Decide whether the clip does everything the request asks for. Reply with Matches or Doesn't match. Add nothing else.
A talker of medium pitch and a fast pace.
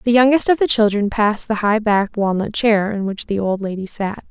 Doesn't match